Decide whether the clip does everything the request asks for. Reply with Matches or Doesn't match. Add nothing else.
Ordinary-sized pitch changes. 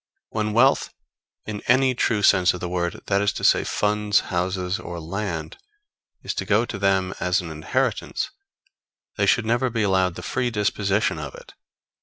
Matches